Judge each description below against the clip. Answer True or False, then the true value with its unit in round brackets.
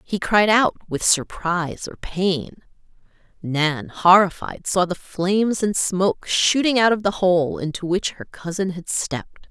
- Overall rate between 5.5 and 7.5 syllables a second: False (4.1 syllables/s)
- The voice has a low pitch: False (185 Hz)